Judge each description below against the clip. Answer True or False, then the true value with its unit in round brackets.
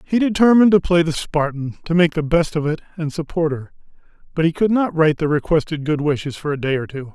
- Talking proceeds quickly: True (245 wpm)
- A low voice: False (160 Hz)